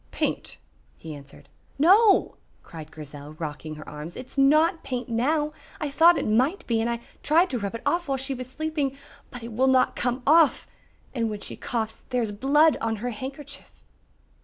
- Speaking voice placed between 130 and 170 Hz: No, very high, 255 Hz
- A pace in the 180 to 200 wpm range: Yes, average, 190 wpm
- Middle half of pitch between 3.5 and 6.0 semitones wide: Yes, wide, 5.5 semitones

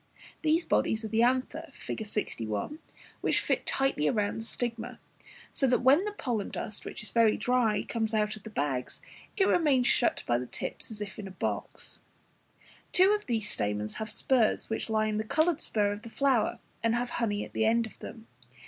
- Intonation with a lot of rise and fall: No, average, 3.3 semitones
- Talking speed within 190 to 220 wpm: Yes, average, 200 wpm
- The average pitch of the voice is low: No, high, 225 Hz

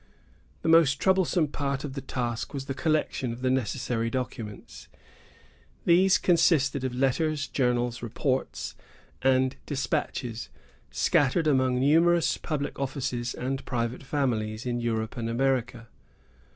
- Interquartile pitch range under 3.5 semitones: Yes, average, 3.1 semitones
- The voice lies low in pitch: Yes, low, 130 Hz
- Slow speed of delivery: Yes, slow, 125 wpm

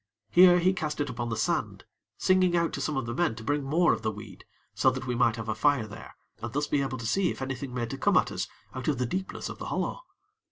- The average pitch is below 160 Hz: Yes, low, 135 Hz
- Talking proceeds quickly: Yes, fast, 275 wpm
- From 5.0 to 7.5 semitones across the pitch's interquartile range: Yes, wide, 5.4 semitones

